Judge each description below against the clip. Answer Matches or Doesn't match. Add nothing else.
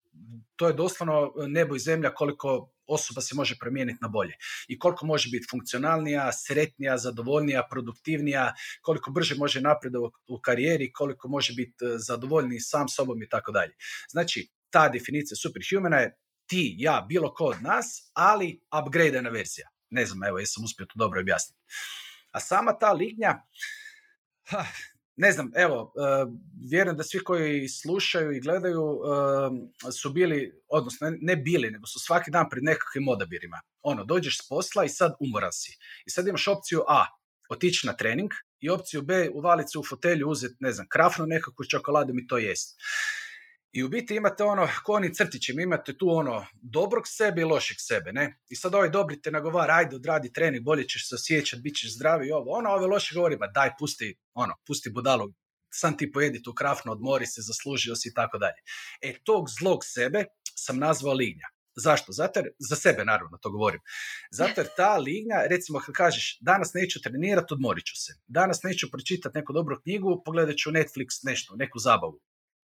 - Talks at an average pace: Doesn't match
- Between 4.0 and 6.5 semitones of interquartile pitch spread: Matches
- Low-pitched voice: Doesn't match